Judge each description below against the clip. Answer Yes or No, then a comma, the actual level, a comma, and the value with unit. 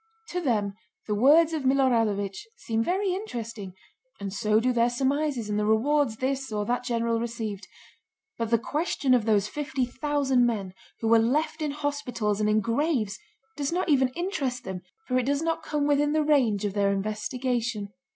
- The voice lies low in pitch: No, high, 245 Hz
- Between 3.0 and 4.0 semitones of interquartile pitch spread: No, average, 5.1 semitones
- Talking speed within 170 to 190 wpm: Yes, average, 180 wpm